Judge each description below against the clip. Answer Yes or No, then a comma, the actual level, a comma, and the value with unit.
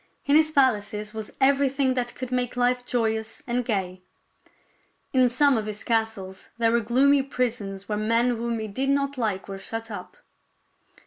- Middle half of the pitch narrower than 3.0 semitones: No, average, 3.3 semitones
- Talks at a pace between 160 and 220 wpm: Yes, average, 170 wpm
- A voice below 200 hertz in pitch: No, high, 235 Hz